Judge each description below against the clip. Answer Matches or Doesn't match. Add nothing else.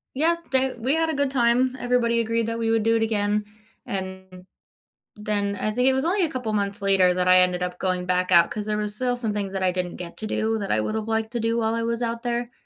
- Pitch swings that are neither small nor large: Matches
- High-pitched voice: Matches